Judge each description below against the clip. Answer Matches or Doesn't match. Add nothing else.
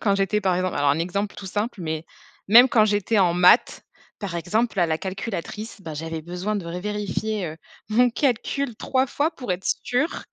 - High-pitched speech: Matches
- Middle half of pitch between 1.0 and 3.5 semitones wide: Doesn't match